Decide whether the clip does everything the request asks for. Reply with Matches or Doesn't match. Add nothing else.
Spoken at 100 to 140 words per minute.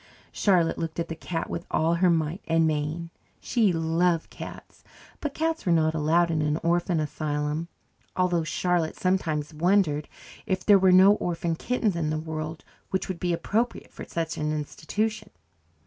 Doesn't match